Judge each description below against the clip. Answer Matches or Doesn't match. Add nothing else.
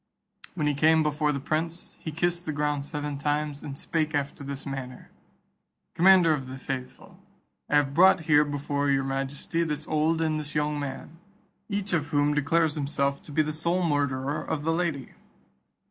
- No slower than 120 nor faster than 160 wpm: Doesn't match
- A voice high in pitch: Doesn't match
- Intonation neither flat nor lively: Doesn't match